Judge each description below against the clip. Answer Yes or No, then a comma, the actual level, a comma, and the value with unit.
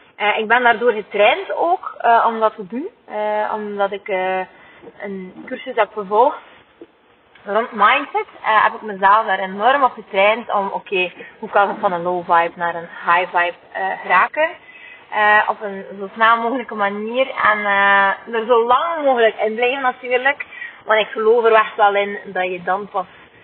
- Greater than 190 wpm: No, average, 180 wpm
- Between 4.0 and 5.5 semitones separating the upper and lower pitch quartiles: No, average, 3.5 semitones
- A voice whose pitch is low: No, high, 215 Hz